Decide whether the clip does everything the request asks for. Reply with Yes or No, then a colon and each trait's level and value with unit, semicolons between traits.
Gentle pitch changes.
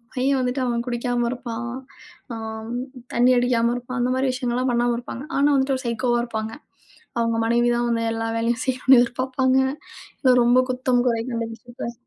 Yes: narrow, 1.4 semitones